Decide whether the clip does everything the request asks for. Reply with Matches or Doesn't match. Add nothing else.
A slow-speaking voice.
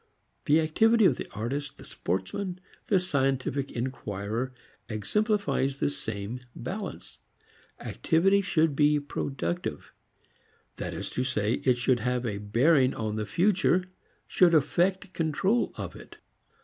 Matches